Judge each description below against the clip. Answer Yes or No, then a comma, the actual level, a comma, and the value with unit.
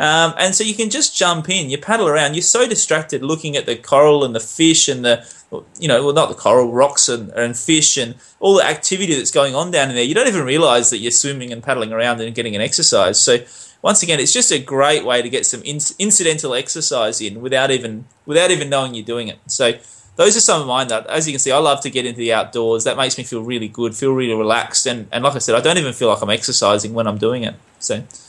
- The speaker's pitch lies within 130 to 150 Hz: Yes, low, 135 Hz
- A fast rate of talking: Yes, fast, 265 wpm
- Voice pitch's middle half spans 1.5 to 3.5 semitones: No, average, 4.9 semitones